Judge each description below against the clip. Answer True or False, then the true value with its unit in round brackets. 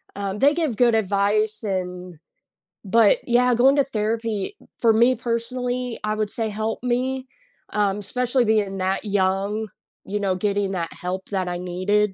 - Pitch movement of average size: True (3.6 semitones)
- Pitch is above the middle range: True (215 Hz)